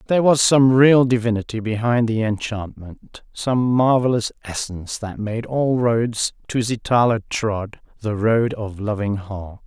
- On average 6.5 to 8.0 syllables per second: No, 4.2 syllables/s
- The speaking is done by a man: Yes, male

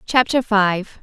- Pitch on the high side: Yes, high, 215 Hz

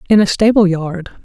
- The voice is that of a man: No, female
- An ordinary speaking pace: Yes, average, 195 wpm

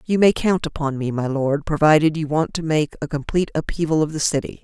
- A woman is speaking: Yes, female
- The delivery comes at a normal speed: No, fast, 235 wpm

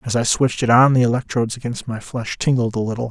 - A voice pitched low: Yes, low, 120 Hz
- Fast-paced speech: Yes, fast, 250 wpm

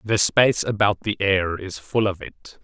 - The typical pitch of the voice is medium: No, low, 100 Hz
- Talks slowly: No, fast, 205 wpm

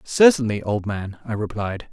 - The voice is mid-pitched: No, low, 115 Hz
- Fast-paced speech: No, average, 155 wpm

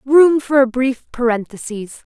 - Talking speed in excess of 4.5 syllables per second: No, 4.1 syllables/s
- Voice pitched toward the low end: No, very high, 255 Hz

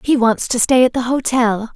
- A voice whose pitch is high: Yes, high, 245 Hz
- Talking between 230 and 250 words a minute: Yes, fast, 240 wpm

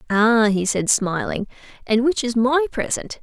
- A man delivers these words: No, female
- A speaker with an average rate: Yes, average, 165 wpm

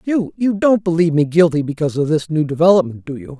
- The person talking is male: Yes, male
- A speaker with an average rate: No, fast, 210 wpm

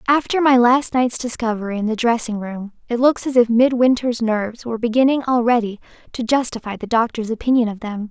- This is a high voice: Yes, high, 235 Hz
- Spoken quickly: No, average, 185 wpm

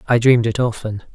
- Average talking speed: No, fast, 210 wpm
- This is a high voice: No, low, 115 Hz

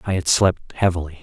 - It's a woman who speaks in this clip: No, male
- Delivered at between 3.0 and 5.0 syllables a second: No, 5.6 syllables/s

